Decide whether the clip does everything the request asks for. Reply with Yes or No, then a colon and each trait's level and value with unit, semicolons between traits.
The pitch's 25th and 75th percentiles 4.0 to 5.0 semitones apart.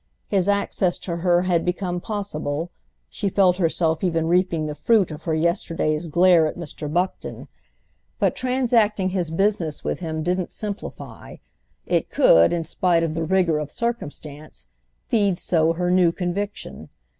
No: average, 3.1 semitones